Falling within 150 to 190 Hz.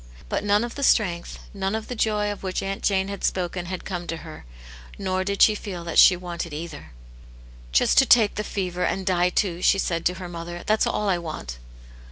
Yes: medium, 185 Hz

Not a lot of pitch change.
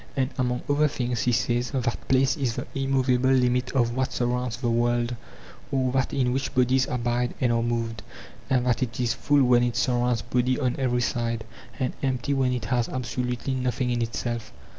Yes: narrow, 1.4 semitones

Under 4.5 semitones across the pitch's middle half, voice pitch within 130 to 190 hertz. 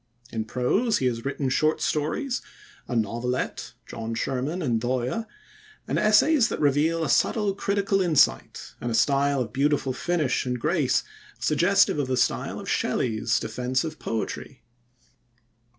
No: wide, 5.5 semitones; medium, 140 Hz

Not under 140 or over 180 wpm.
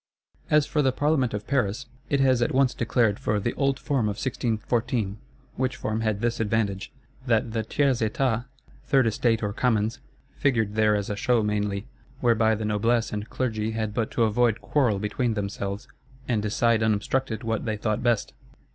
Yes: average, 175 wpm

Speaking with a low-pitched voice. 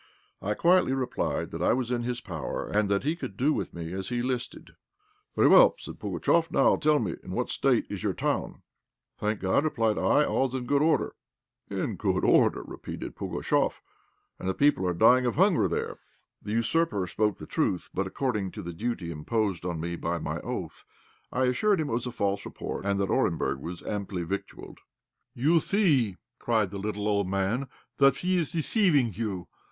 Yes: low, 115 Hz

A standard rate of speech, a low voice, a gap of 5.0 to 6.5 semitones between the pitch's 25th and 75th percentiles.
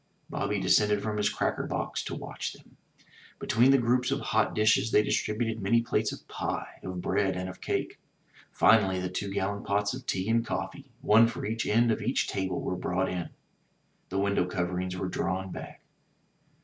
No: average, 190 wpm; low, 100 Hz; average, 3.3 semitones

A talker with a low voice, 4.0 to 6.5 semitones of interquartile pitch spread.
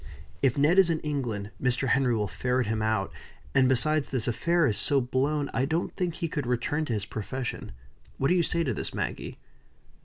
Yes: low, 130 Hz; average, 4.3 semitones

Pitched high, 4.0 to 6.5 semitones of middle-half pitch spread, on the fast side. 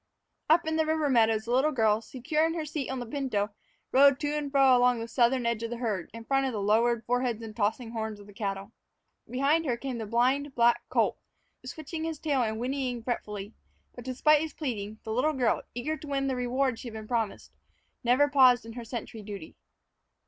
No: high, 245 Hz; average, 3.6 semitones; fast, 215 wpm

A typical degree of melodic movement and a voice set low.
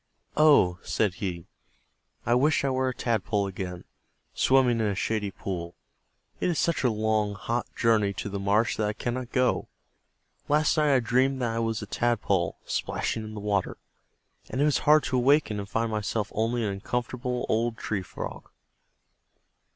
Yes: average, 3.7 semitones; low, 115 Hz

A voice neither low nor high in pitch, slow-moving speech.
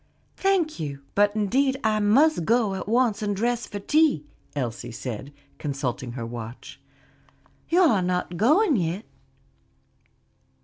No: high, 205 Hz; slow, 130 wpm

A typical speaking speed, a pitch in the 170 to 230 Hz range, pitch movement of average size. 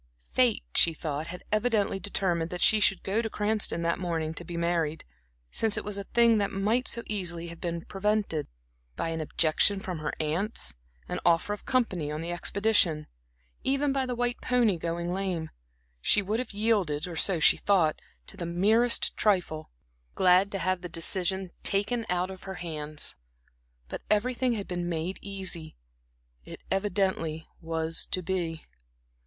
Yes: average, 170 wpm; medium, 185 Hz; average, 3.9 semitones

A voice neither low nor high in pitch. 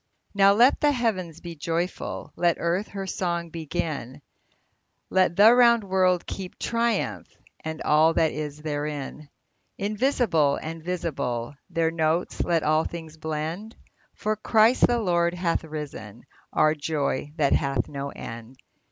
Yes: medium, 165 Hz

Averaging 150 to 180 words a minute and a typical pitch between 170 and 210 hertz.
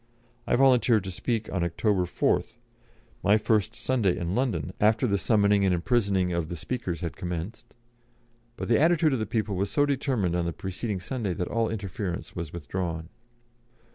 No: average, 170 wpm; low, 100 Hz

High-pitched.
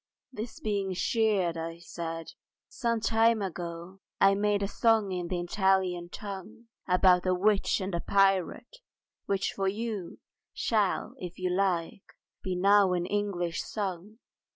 Yes: high, 195 Hz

